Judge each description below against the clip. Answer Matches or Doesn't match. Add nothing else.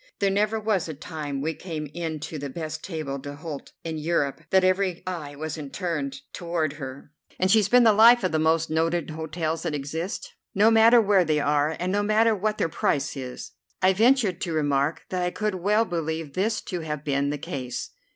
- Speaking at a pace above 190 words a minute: Matches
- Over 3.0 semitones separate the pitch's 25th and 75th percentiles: Matches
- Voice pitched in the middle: Matches